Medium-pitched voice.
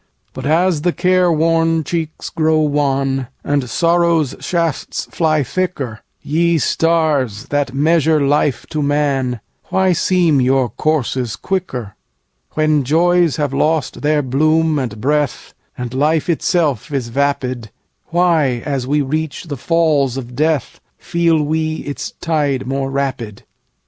Yes: medium, 150 Hz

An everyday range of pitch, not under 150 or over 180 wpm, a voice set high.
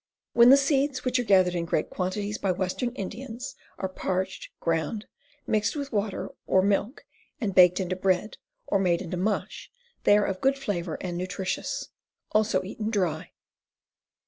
Yes: average, 3.5 semitones; average, 160 wpm; high, 195 Hz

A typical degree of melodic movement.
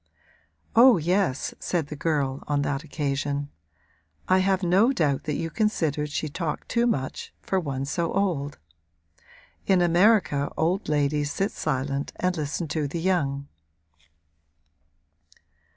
Yes: average, 4.5 semitones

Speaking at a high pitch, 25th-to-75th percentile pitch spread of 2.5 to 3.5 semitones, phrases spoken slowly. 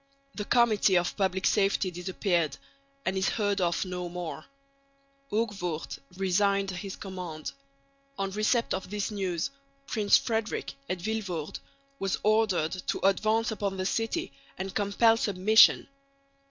Yes: high, 195 Hz; average, 2.8 semitones; slow, 125 wpm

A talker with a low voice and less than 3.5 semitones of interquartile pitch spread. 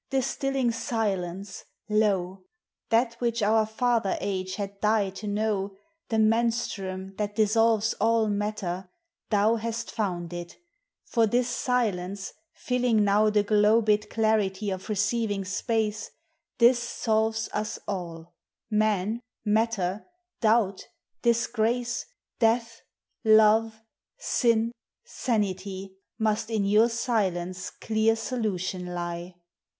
No: high, 215 Hz; average, 2.7 semitones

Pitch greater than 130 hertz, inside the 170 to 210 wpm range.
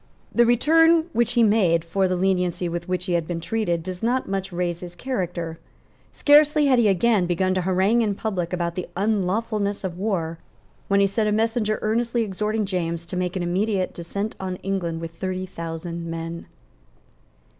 Yes: high, 190 Hz; average, 180 wpm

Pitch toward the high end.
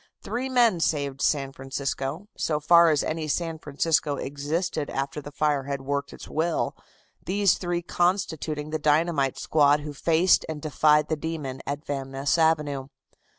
No: medium, 150 Hz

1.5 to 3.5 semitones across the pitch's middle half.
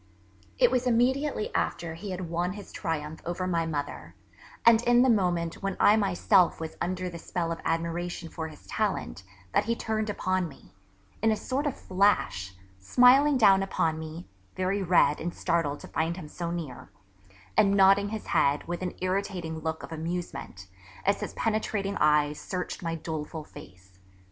No: average, 3.9 semitones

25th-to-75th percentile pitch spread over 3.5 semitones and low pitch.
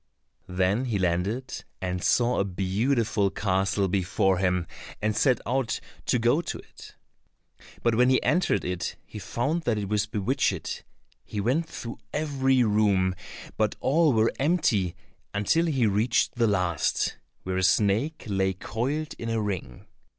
Yes: average, 5.0 semitones; low, 105 Hz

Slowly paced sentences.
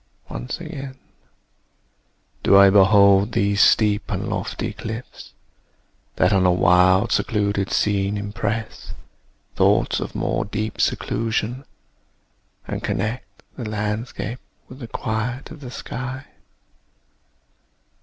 Yes: slow, 105 wpm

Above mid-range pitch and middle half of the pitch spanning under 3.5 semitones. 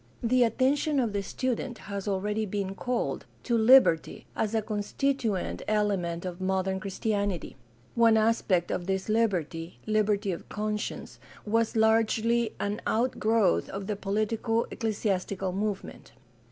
Yes: high, 210 Hz; average, 2.8 semitones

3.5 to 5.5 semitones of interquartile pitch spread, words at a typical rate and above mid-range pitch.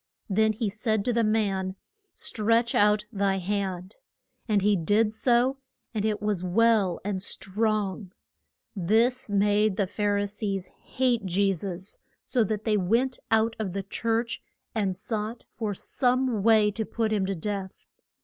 No: narrow, 2.5 semitones; average, 155 wpm; high, 210 Hz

